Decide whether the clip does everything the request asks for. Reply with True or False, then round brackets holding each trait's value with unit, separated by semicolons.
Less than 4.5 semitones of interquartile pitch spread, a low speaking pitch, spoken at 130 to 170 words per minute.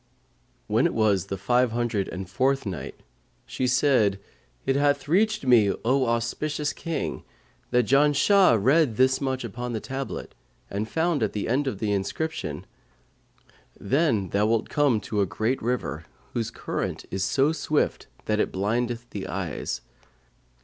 False (5.1 semitones; 120 Hz; 150 wpm)